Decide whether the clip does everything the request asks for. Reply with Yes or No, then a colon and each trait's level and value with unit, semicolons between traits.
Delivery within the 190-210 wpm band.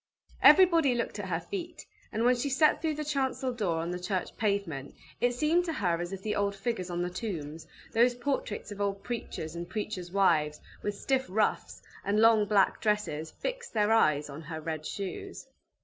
Yes: average, 195 wpm